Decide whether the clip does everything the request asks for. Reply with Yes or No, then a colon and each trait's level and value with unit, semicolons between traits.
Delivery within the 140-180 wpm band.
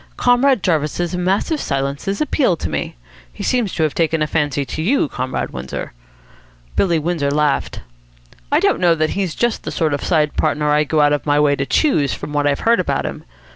No: fast, 205 wpm